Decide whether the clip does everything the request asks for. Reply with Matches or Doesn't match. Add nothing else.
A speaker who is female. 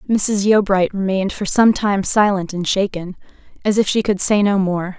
Matches